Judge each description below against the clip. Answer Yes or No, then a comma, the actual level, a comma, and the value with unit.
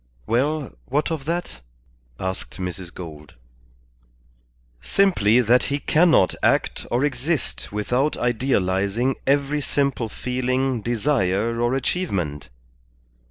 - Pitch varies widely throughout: Yes, wide, 6.1 semitones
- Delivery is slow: Yes, slow, 100 wpm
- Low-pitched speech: Yes, low, 125 Hz